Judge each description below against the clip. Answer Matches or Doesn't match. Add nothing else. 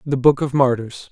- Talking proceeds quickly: Matches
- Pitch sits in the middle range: Doesn't match